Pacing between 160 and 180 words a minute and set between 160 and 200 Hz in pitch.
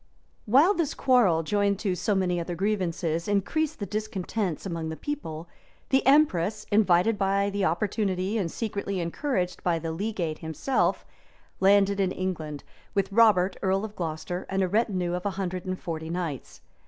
Yes: average, 165 wpm; high, 190 Hz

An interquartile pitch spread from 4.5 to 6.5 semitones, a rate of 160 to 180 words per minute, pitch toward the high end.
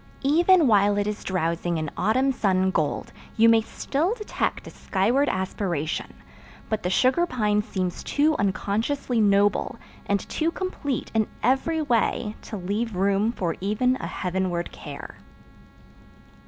No: wide, 5.4 semitones; average, 140 wpm; high, 210 Hz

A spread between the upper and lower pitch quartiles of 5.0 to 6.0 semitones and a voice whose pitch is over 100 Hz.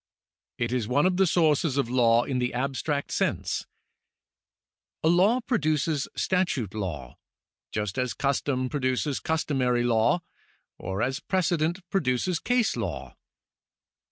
Yes: wide, 5.5 semitones; medium, 140 Hz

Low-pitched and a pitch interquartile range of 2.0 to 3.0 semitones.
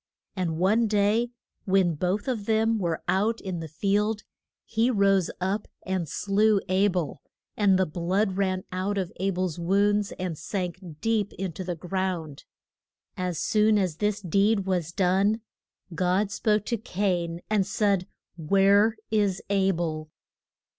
No: high, 195 Hz; narrow, 2.5 semitones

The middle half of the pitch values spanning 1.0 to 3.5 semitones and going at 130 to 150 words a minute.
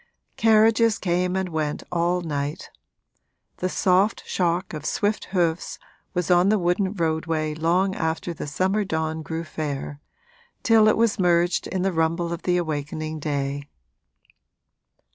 Yes: average, 3.0 semitones; average, 140 wpm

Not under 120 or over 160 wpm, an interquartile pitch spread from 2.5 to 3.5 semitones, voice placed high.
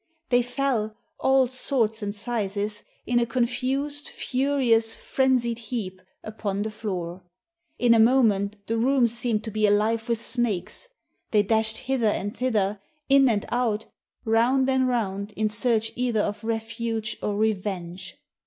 Yes: average, 145 wpm; average, 2.8 semitones; high, 225 Hz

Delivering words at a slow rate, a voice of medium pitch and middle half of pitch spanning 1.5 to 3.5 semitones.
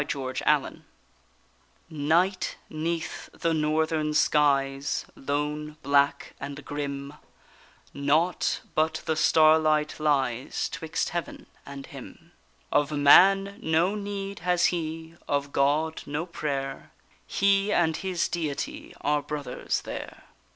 Yes: slow, 110 wpm; medium, 155 Hz; average, 2.9 semitones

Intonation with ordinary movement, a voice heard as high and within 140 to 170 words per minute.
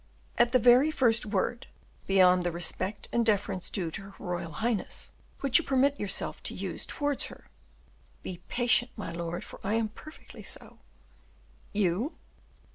Yes: average, 4.9 semitones; high, 215 Hz; average, 155 wpm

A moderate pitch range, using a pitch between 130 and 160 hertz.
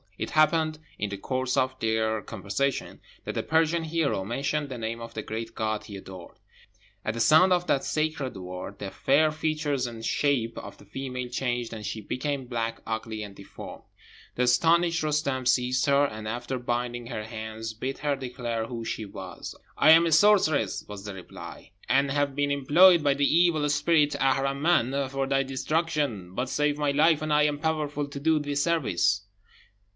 Yes: average, 4.8 semitones; low, 135 Hz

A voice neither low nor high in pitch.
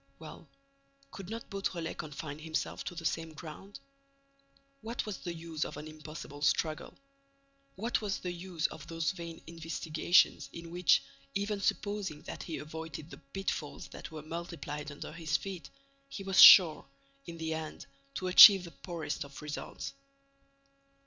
Yes: medium, 165 Hz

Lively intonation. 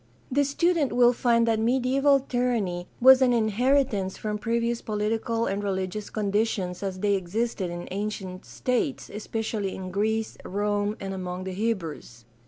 No: average, 3.8 semitones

